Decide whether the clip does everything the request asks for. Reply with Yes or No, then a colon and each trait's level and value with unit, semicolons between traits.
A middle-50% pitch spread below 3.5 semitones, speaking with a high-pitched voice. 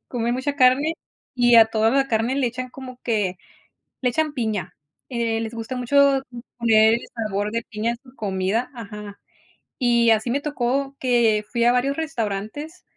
Yes: average, 2.9 semitones; high, 235 Hz